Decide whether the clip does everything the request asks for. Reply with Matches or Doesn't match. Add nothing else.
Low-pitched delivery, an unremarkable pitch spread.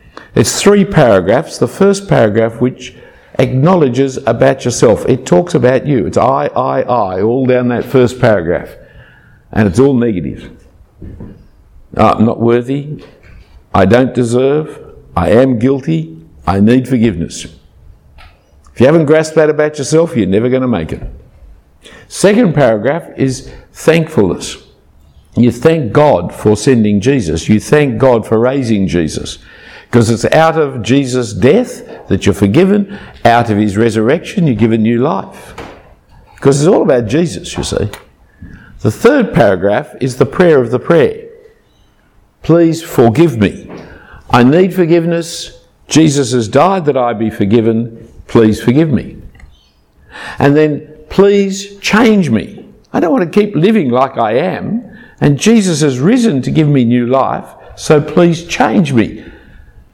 Doesn't match